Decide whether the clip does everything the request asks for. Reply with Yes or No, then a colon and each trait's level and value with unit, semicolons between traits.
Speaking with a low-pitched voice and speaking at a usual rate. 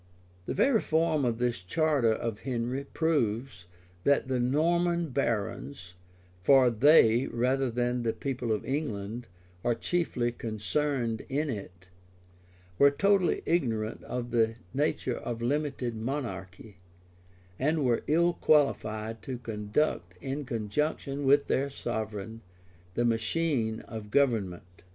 No: low, 120 Hz; slow, 120 wpm